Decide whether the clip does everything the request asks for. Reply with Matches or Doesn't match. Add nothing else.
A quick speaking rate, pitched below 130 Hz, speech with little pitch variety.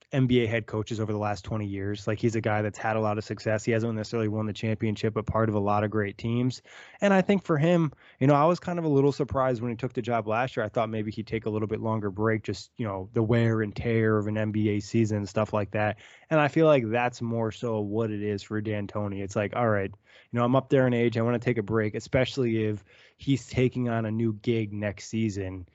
Matches